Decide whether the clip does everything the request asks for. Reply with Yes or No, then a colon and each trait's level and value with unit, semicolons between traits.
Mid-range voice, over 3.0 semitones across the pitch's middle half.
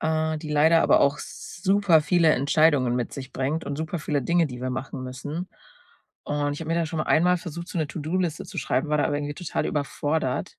No: medium, 155 Hz; narrow, 2.5 semitones